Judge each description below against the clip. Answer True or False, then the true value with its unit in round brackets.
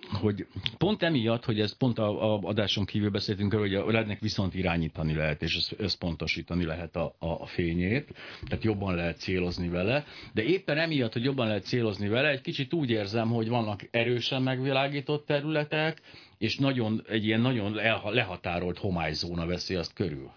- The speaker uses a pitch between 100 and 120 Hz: True (110 Hz)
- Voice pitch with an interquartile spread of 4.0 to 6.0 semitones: True (5.1 semitones)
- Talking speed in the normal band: False (160 wpm)